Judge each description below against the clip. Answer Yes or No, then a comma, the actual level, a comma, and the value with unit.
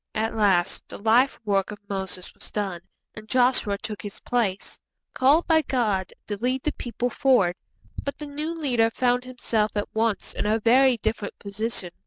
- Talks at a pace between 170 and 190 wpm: Yes, average, 175 wpm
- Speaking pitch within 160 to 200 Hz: No, high, 225 Hz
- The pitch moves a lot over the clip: No, average, 3.8 semitones